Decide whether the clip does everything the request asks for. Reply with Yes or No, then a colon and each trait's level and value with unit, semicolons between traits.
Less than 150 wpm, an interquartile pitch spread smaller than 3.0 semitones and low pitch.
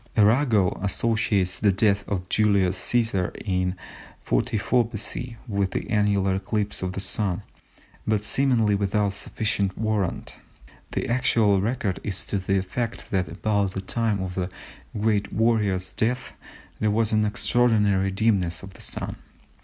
Yes: average, 140 wpm; narrow, 2.5 semitones; low, 100 Hz